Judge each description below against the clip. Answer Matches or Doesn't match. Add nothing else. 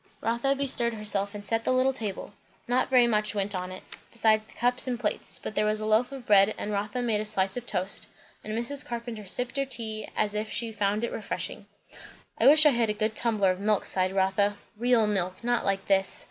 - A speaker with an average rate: Doesn't match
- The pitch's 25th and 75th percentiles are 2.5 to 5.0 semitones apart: Matches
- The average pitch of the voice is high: Matches